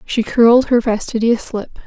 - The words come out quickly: No, average, 160 wpm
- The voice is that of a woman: Yes, female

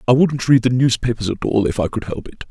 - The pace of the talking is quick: Yes, fast, 285 wpm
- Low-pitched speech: Yes, low, 120 Hz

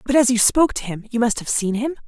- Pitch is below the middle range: No, high, 240 Hz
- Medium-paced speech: No, fast, 320 wpm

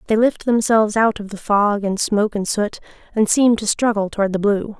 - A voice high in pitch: Yes, high, 210 Hz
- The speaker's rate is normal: No, fast, 225 wpm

